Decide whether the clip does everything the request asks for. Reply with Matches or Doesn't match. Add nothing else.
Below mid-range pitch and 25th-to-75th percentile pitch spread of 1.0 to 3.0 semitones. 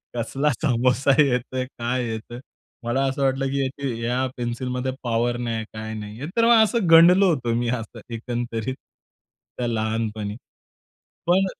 Matches